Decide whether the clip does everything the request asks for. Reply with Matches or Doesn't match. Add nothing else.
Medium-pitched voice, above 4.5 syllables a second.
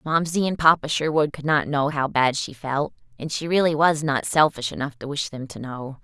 Matches